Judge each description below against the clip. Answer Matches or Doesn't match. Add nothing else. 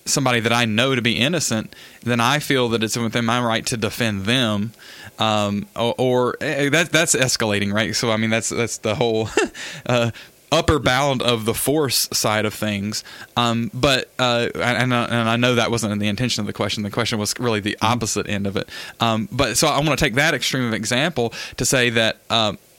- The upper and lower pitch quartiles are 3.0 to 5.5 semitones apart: Doesn't match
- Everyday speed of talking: Doesn't match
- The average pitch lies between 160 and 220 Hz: Doesn't match